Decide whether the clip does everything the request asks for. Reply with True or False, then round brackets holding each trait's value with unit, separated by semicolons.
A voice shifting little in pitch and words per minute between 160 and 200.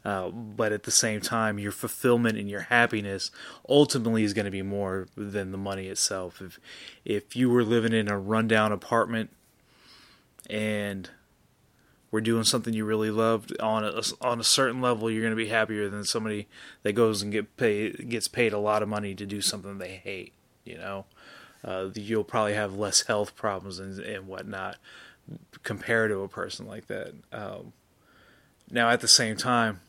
True (2.2 semitones; 180 wpm)